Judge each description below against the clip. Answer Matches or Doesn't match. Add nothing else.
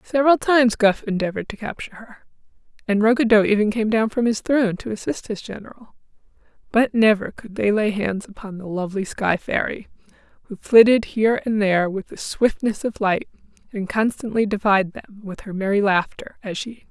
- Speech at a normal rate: Matches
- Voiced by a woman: Matches